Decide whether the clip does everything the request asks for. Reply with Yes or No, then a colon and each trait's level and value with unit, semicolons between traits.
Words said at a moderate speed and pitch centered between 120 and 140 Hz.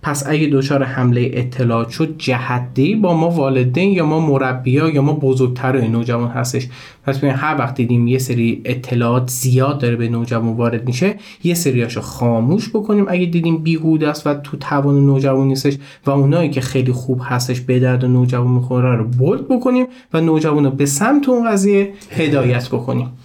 No: fast, 170 wpm; low, 135 Hz